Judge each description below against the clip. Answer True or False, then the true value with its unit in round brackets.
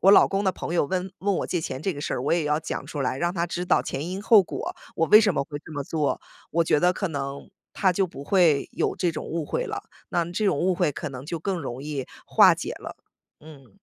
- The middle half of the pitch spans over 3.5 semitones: True (4.3 semitones)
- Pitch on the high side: False (170 Hz)